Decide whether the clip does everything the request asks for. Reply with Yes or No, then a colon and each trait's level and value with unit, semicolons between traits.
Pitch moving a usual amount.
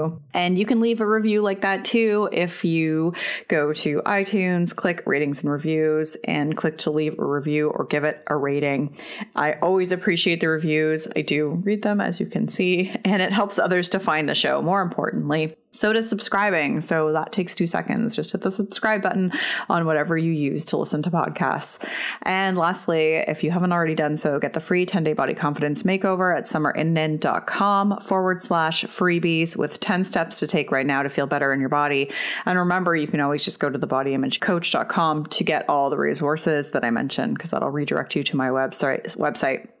Yes: average, 4.3 semitones